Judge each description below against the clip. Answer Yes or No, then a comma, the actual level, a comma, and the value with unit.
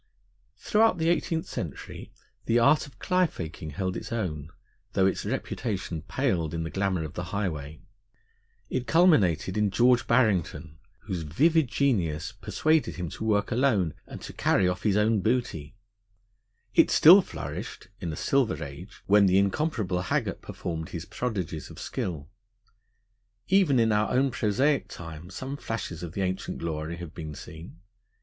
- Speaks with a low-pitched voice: Yes, very low, 95 Hz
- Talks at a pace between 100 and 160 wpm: Yes, average, 155 wpm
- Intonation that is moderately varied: No, wide, 6.9 semitones